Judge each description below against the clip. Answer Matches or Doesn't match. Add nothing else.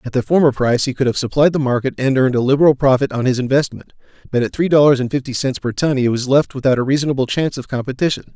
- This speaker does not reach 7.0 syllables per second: Doesn't match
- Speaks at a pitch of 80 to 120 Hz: Doesn't match